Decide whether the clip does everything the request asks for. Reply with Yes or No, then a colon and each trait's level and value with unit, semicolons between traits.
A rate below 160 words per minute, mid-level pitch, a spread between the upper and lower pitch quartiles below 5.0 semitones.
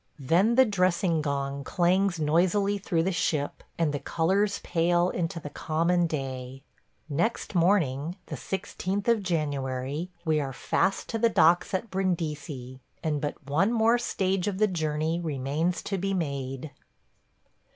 Yes: average, 145 wpm; medium, 170 Hz; average, 4.6 semitones